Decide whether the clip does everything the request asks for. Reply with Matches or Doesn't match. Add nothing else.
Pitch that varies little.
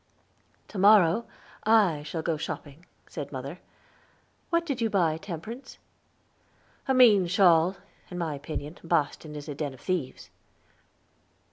Doesn't match